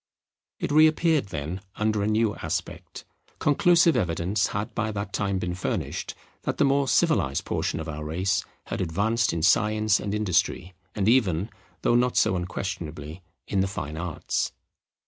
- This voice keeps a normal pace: Yes, average, 160 wpm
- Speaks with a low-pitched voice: Yes, low, 100 Hz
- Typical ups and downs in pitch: Yes, average, 4.5 semitones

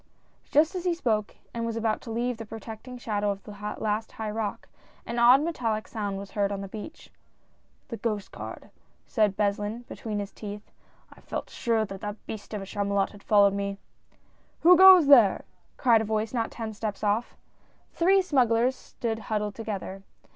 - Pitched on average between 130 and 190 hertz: No, high, 220 Hz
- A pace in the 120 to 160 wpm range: No, average, 195 wpm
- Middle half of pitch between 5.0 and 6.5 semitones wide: No, narrow, 2.5 semitones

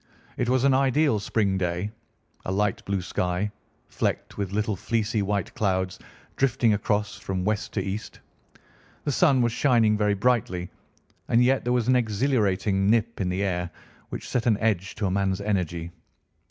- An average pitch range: Yes, average, 3.7 semitones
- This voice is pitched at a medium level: No, low, 105 Hz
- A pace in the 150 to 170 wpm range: Yes, average, 165 wpm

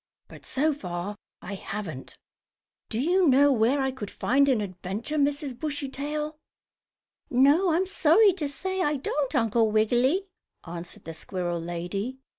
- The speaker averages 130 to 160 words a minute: Yes, average, 140 wpm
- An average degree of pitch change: No, wide, 6.6 semitones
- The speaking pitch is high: Yes, very high, 265 Hz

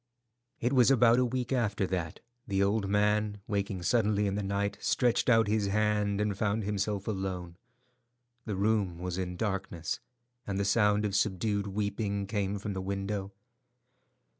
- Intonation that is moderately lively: No, narrow, 1.6 semitones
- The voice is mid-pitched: No, low, 100 Hz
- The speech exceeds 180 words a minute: No, average, 160 wpm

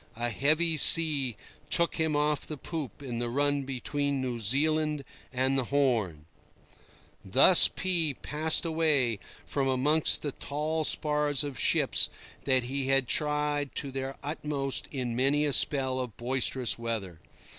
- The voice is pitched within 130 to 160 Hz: Yes, medium, 140 Hz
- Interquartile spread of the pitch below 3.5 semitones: Yes, average, 2.8 semitones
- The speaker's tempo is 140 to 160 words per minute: Yes, average, 145 wpm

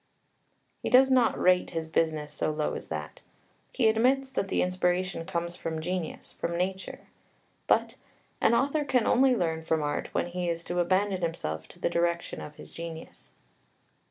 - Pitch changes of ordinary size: Yes, average, 4.0 semitones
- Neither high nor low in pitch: Yes, medium, 175 Hz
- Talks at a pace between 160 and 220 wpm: Yes, average, 170 wpm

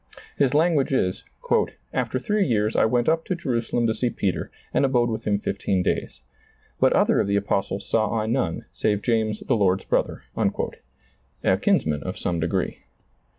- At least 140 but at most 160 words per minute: No, average, 170 wpm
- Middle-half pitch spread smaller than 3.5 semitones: No, average, 4.5 semitones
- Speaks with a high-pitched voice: No, low, 110 Hz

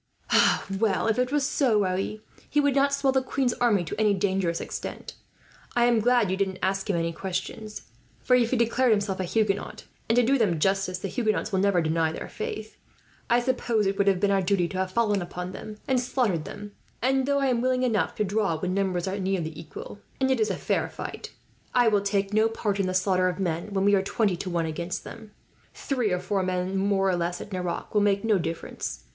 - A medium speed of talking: No, fast, 230 wpm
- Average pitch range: Yes, average, 3.9 semitones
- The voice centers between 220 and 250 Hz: No, high, 200 Hz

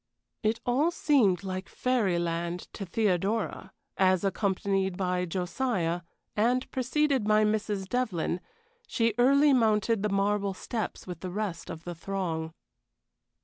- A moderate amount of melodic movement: Yes, average, 4.1 semitones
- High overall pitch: Yes, high, 200 Hz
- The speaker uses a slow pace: Yes, slow, 130 wpm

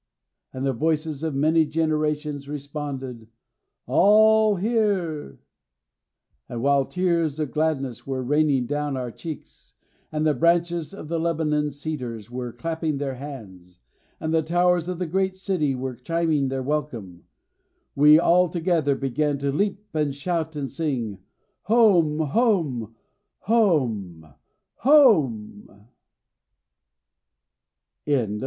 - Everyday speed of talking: No, slow, 115 wpm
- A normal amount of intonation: Yes, average, 4.1 semitones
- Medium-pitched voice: Yes, medium, 150 Hz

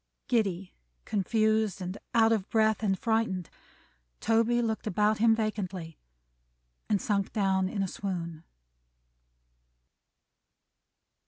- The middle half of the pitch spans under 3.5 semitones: Yes, average, 2.8 semitones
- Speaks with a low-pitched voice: No, high, 210 Hz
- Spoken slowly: Yes, slow, 100 wpm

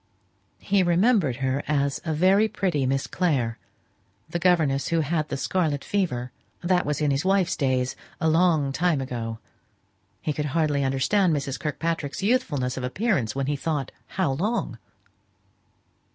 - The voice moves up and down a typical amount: Yes, average, 4.7 semitones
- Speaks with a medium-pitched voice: Yes, medium, 150 Hz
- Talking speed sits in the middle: Yes, average, 150 wpm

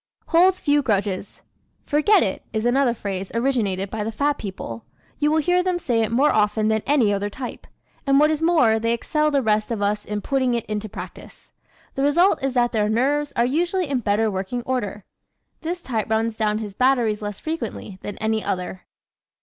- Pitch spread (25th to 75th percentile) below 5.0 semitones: No, wide, 5.5 semitones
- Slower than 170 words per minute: No, average, 200 wpm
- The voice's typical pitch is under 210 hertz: No, high, 230 Hz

